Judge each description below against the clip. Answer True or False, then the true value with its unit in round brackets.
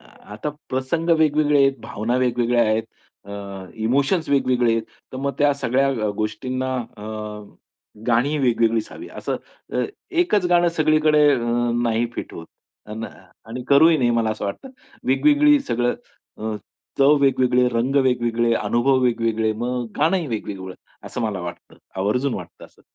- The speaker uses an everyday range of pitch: True (4.1 semitones)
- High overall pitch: False (125 Hz)